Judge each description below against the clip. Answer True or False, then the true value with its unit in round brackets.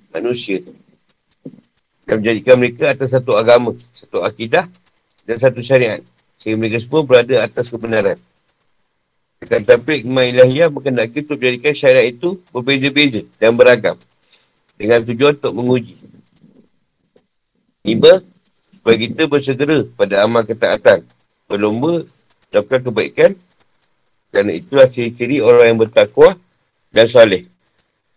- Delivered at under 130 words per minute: True (110 wpm)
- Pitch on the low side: True (130 Hz)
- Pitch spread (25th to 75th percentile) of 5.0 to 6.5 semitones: True (5.4 semitones)